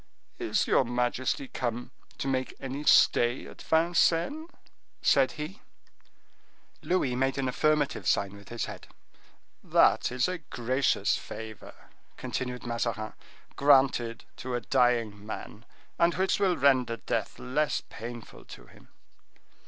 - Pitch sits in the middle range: No, low, 130 Hz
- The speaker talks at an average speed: No, slow, 125 wpm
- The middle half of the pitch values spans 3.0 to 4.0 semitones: Yes, average, 3.7 semitones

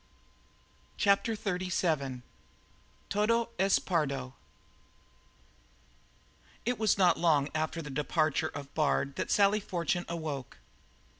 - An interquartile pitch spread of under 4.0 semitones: No, wide, 5.4 semitones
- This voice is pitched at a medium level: Yes, medium, 170 Hz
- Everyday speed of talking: No, slow, 95 wpm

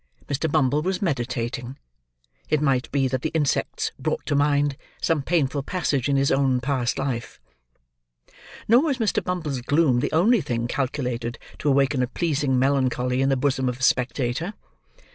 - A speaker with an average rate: Yes, average, 160 wpm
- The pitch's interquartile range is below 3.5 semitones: Yes, average, 3.0 semitones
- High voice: No, low, 135 Hz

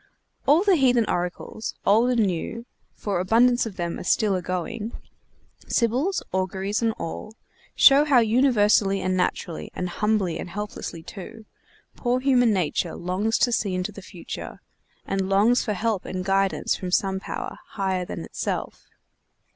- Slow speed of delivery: No, average, 150 wpm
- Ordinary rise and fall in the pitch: Yes, average, 4.0 semitones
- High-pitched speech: Yes, high, 205 Hz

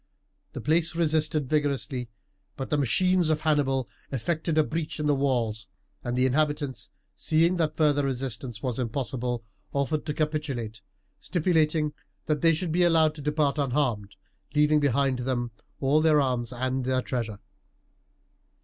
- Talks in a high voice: No, medium, 145 Hz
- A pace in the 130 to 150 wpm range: Yes, average, 145 wpm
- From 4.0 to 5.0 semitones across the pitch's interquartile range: No, average, 3.5 semitones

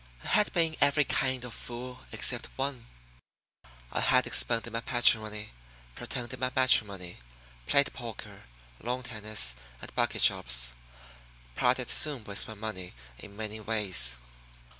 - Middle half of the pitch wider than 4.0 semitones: No, average, 3.5 semitones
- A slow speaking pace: Yes, slow, 130 wpm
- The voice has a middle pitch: No, low, 115 Hz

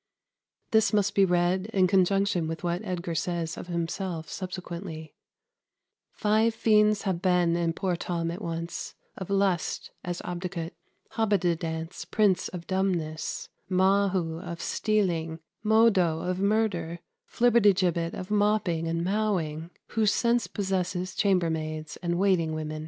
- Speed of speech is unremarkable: No, slow, 130 wpm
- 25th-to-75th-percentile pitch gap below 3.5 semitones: Yes, average, 3.0 semitones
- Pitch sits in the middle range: Yes, medium, 180 Hz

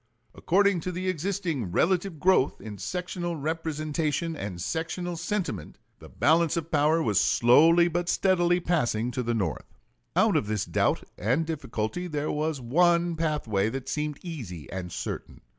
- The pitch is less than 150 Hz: No, medium, 160 Hz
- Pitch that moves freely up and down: Yes, wide, 6.0 semitones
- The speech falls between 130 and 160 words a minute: Yes, average, 150 wpm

